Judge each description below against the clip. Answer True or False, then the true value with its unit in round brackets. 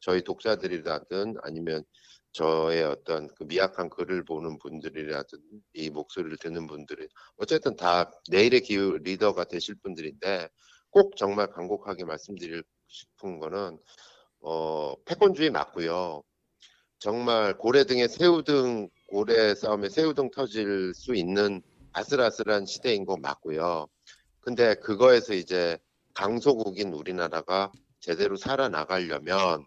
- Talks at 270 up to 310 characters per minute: True (285 characters per minute)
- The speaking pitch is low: True (95 Hz)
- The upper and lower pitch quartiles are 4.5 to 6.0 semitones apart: True (5.4 semitones)